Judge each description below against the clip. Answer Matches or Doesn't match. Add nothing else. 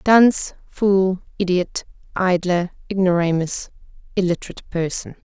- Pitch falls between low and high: Matches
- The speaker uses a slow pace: Matches